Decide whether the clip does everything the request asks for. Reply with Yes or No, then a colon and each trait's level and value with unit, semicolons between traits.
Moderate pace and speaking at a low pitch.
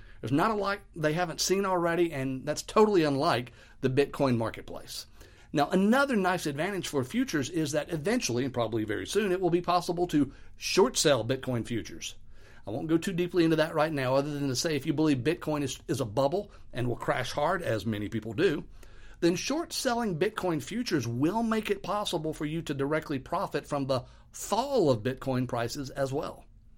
No: average, 195 wpm; medium, 150 Hz